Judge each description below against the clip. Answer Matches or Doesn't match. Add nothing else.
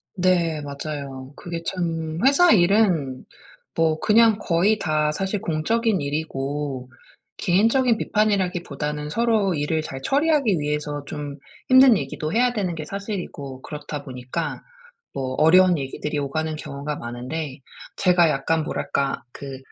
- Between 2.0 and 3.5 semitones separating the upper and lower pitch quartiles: Doesn't match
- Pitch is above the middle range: Doesn't match